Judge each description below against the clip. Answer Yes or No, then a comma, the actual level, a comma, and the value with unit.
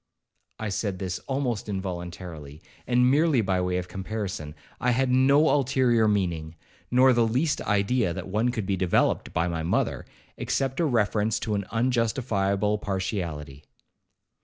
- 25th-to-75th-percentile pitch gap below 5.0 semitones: No, wide, 5.4 semitones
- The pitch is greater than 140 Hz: No, low, 105 Hz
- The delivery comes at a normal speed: Yes, average, 145 wpm